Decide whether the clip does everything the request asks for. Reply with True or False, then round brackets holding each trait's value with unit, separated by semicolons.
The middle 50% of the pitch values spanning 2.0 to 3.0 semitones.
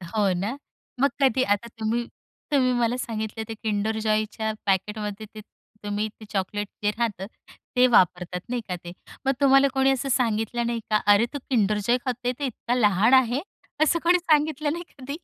False (3.8 semitones)